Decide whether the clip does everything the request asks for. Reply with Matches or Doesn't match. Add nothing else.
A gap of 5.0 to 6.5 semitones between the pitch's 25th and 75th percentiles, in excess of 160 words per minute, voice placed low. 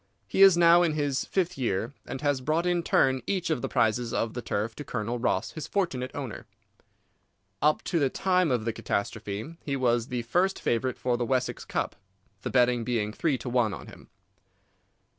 Matches